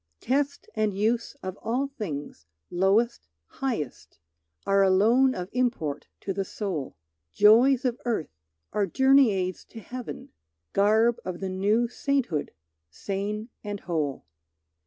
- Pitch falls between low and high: No, high, 210 Hz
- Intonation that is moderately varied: Yes, average, 4.5 semitones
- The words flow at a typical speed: No, slow, 125 wpm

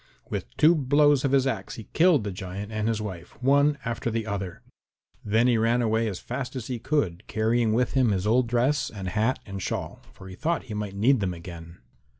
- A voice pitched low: Yes, low, 115 Hz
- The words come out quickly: Yes, fast, 215 wpm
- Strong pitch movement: No, average, 4.5 semitones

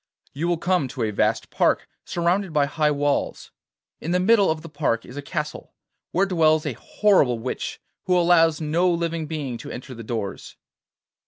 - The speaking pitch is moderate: Yes, medium, 155 Hz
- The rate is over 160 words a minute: Yes, average, 180 wpm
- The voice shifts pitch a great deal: No, average, 3.7 semitones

